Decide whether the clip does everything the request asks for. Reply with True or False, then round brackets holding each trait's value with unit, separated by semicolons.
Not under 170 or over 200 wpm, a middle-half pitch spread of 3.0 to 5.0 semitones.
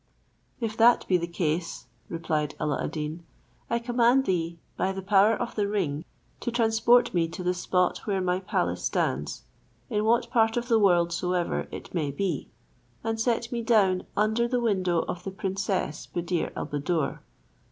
True (175 wpm; 4.7 semitones)